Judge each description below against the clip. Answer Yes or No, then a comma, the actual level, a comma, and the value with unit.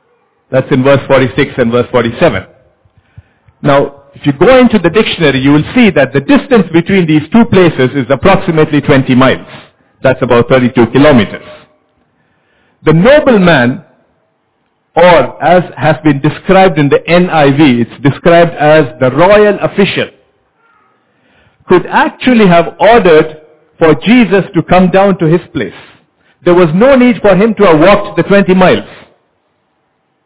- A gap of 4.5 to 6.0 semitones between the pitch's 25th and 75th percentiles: Yes, wide, 5.6 semitones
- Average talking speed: Yes, average, 145 wpm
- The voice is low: No, medium, 160 Hz